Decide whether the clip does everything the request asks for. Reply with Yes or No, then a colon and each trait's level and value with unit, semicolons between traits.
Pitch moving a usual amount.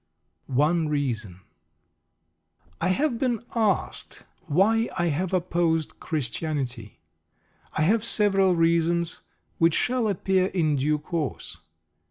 Yes: average, 4.3 semitones